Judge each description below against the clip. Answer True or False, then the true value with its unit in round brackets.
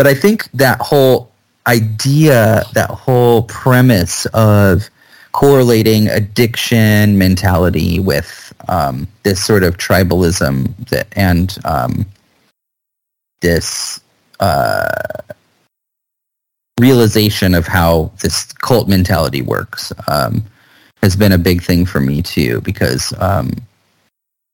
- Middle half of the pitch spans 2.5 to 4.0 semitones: False (4.5 semitones)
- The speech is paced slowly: True (105 wpm)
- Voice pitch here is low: True (105 Hz)